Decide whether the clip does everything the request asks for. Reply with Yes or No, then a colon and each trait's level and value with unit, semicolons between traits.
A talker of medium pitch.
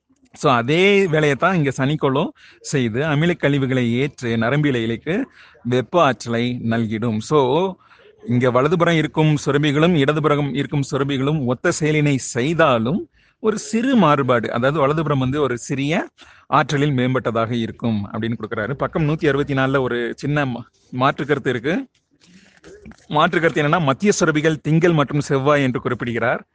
Yes: medium, 145 Hz